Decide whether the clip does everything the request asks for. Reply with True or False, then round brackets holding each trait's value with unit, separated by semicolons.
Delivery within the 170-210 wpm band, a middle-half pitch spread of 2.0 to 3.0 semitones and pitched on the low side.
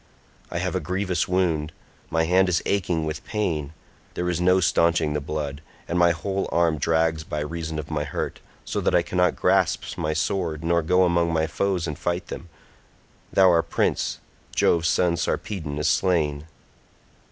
True (175 wpm; 2.5 semitones; 85 Hz)